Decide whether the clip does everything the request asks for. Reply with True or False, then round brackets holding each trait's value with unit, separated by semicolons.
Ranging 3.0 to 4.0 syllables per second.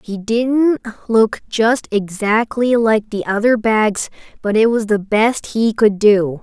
True (3.6 syllables/s)